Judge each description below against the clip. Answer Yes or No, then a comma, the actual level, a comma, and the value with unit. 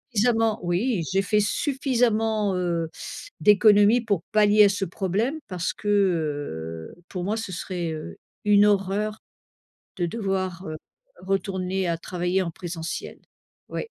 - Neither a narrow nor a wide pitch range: Yes, average, 3.1 semitones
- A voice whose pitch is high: Yes, high, 195 Hz